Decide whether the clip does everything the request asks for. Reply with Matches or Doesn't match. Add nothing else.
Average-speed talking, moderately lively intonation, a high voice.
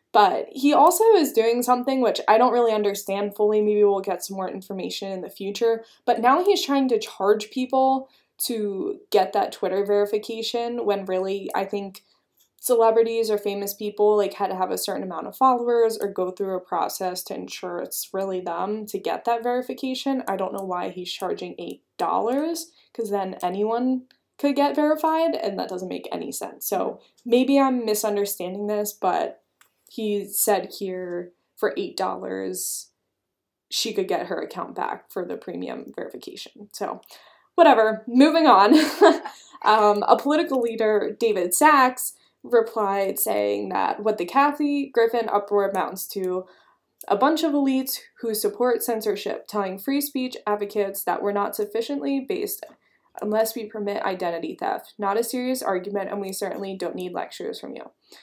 Matches